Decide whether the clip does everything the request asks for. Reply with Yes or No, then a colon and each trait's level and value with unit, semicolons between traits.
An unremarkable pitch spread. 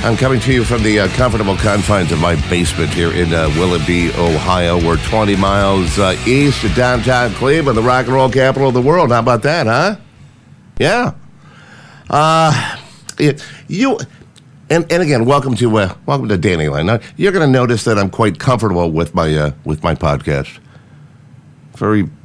No: wide, 7.1 semitones